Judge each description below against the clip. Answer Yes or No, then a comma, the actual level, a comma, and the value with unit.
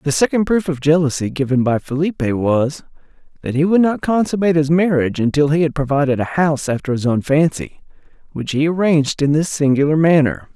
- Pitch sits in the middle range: Yes, medium, 150 Hz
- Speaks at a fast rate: No, average, 190 wpm